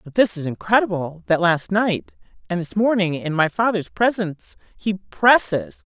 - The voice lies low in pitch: No, high, 190 Hz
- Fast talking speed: No, average, 160 wpm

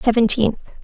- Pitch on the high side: Yes, high, 225 Hz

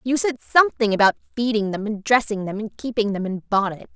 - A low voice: No, high, 220 Hz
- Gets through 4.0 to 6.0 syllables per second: No, 6.2 syllables/s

